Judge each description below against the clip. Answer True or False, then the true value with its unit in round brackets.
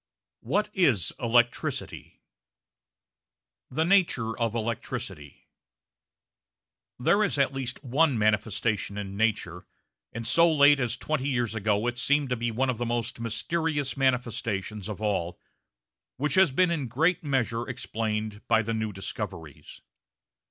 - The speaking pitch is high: False (120 Hz)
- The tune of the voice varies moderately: True (4.5 semitones)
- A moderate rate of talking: False (130 wpm)